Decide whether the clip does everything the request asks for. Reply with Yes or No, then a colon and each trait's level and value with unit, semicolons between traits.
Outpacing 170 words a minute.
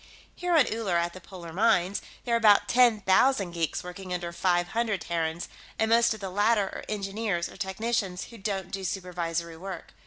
Yes: average, 190 wpm